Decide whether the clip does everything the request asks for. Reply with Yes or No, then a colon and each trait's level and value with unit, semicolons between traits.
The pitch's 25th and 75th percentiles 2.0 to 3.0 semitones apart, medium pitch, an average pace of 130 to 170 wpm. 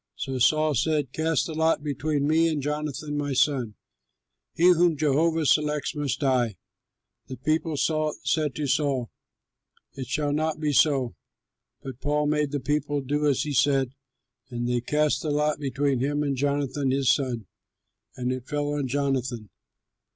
Yes: narrow, 2.4 semitones; medium, 145 Hz; average, 160 wpm